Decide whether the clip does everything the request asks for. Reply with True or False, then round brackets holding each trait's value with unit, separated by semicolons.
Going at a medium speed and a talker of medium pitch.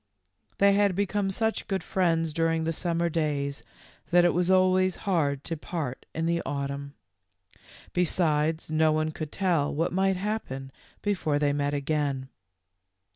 True (145 wpm; 165 Hz)